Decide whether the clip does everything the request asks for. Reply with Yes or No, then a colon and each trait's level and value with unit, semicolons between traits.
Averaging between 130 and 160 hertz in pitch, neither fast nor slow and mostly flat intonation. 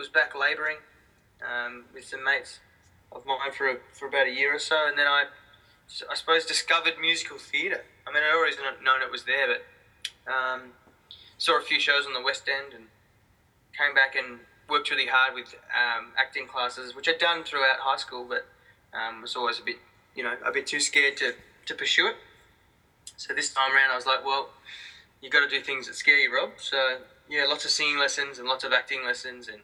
No: low, 135 Hz; fast, 215 wpm; narrow, 2.0 semitones